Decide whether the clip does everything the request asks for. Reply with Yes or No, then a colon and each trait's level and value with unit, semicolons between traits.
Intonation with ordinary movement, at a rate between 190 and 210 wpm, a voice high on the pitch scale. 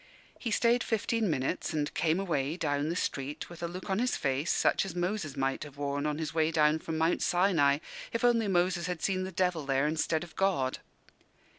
No: average, 4.3 semitones; fast, 205 wpm; medium, 165 Hz